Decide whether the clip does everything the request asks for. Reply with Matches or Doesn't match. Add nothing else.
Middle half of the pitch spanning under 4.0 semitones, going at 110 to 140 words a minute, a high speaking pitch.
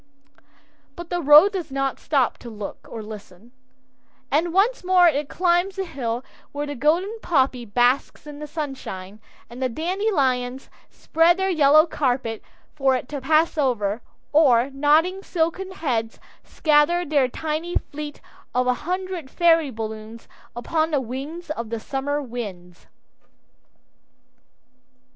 Doesn't match